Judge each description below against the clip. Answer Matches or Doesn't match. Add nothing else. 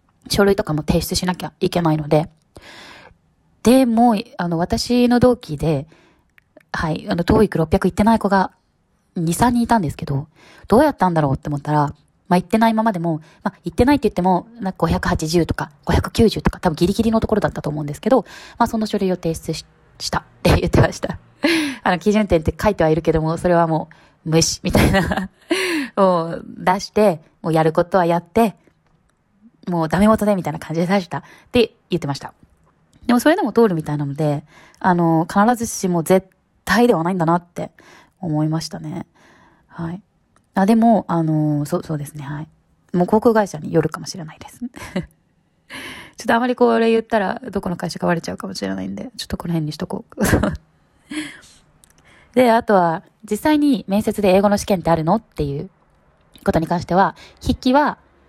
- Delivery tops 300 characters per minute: Matches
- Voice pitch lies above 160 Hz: Matches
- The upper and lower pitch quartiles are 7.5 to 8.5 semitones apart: Doesn't match